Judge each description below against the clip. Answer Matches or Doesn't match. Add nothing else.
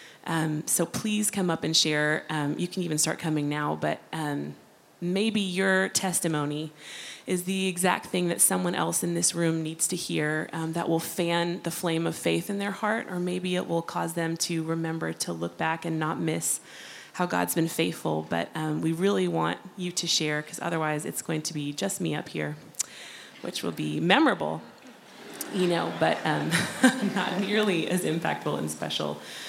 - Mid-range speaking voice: Matches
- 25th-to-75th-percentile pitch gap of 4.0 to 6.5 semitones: Doesn't match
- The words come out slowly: Doesn't match